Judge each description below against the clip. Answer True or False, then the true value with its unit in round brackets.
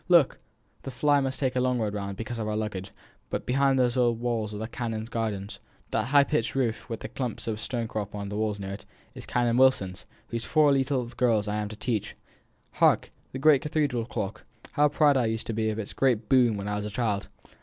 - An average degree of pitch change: True (3.6 semitones)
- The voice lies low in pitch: True (115 Hz)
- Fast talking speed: True (230 wpm)